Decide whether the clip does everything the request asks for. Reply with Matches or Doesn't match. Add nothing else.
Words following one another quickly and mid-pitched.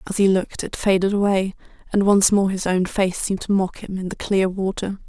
Doesn't match